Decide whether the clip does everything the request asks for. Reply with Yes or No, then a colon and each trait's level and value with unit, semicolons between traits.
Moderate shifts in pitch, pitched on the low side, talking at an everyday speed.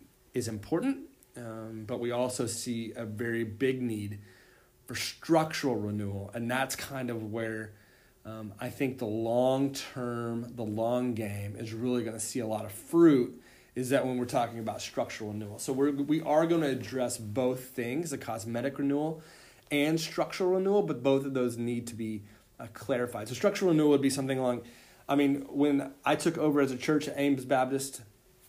Yes: average, 3.6 semitones; low, 125 Hz; average, 185 wpm